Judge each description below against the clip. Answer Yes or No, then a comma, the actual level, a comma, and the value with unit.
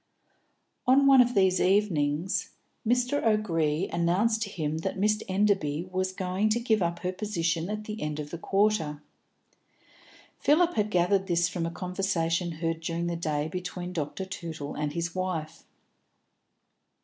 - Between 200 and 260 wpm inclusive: No, average, 150 wpm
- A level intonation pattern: No, average, 4.1 semitones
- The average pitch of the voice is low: No, medium, 180 Hz